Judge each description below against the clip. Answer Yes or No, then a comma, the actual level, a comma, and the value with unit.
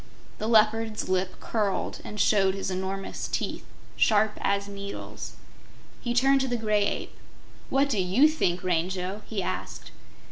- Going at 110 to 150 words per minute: Yes, average, 145 wpm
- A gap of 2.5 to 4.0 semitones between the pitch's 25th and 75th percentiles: Yes, average, 2.9 semitones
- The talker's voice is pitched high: Yes, high, 205 Hz